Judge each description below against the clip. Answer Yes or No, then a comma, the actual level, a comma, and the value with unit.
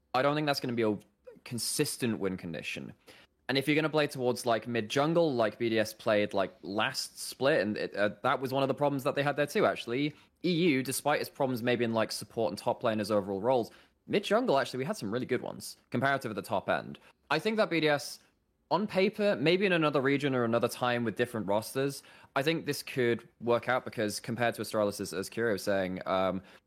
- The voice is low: Yes, low, 125 Hz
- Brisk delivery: Yes, fast, 230 wpm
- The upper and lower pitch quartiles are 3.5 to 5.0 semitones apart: Yes, average, 4.6 semitones